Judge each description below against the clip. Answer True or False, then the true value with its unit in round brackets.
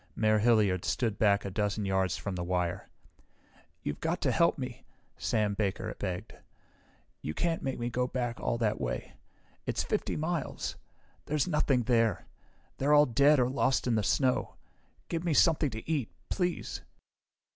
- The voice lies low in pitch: True (115 Hz)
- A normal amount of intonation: False (5.9 semitones)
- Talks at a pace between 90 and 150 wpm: False (160 wpm)